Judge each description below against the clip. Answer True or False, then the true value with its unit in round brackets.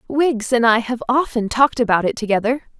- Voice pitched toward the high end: True (240 Hz)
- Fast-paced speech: False (195 wpm)